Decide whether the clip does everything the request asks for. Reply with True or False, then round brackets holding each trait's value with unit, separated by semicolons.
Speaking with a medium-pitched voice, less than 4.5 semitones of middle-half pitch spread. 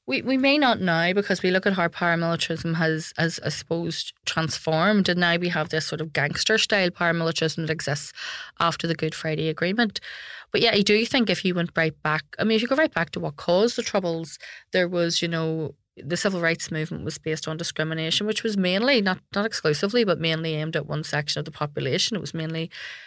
True (165 Hz; 3.6 semitones)